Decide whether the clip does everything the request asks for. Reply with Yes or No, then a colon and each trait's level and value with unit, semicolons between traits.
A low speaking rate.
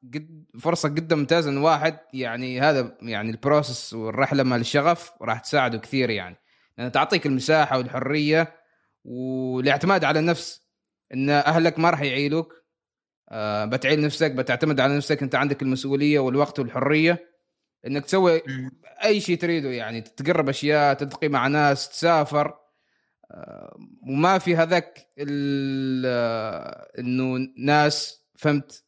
No: average, 115 wpm